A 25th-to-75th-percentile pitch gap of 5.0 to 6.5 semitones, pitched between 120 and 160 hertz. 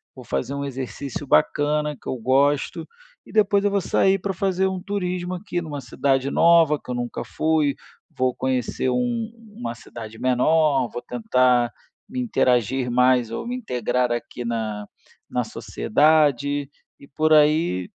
Yes: average, 5.3 semitones; medium, 140 Hz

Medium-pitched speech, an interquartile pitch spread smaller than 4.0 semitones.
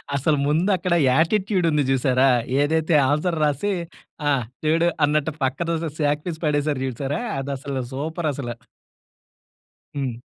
Yes: medium, 150 Hz; average, 2.9 semitones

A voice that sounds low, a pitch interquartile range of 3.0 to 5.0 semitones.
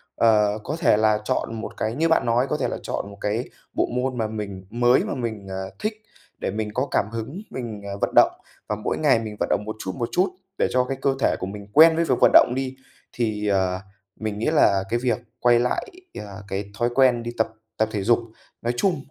Yes: low, 115 Hz; average, 3.4 semitones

